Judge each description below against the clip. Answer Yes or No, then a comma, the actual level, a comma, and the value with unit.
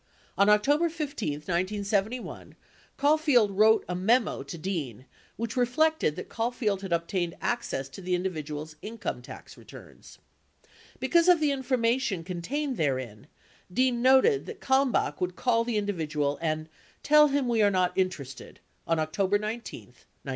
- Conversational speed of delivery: Yes, average, 145 wpm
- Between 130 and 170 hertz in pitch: No, high, 210 Hz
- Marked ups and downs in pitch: Yes, wide, 7.1 semitones